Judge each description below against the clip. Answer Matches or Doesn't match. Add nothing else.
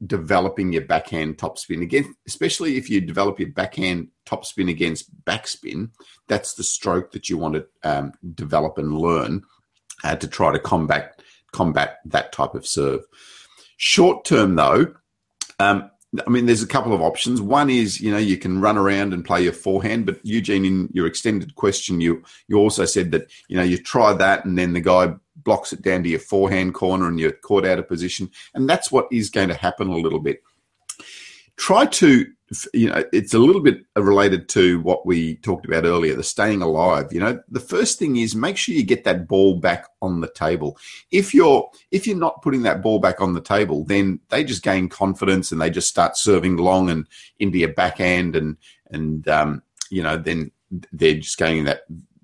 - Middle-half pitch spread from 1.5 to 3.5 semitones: Matches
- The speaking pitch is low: Matches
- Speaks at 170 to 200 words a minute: Matches